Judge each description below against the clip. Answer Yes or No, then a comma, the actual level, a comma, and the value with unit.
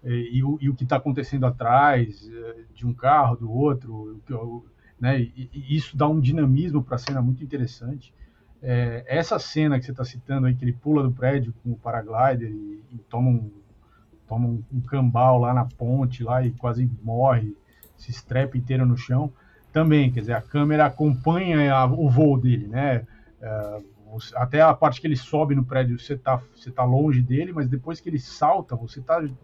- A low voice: Yes, low, 125 Hz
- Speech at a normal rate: No, fast, 190 wpm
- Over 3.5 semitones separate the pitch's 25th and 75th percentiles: No, average, 2.8 semitones